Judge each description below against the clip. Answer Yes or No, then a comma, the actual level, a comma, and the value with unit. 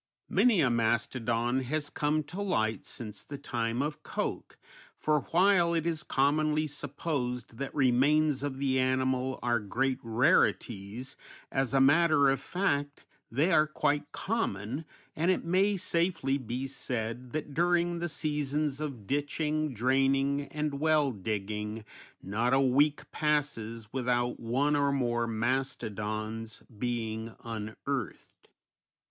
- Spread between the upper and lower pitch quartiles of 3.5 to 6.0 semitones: Yes, average, 4.3 semitones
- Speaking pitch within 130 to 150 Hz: Yes, low, 135 Hz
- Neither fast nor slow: No, slow, 130 wpm